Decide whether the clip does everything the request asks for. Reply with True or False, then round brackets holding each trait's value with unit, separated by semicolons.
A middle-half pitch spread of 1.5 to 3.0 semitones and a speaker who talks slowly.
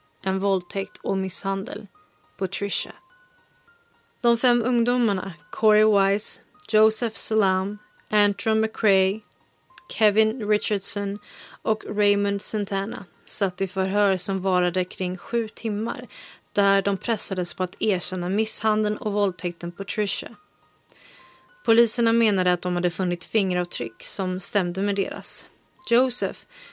True (2.4 semitones; 110 wpm)